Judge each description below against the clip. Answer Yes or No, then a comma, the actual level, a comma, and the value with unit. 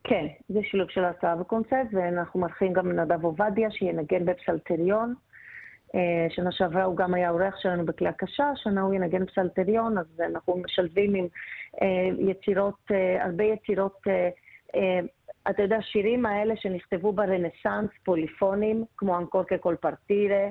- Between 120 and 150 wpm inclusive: Yes, average, 125 wpm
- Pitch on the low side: No, high, 190 Hz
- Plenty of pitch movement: No, narrow, 2.6 semitones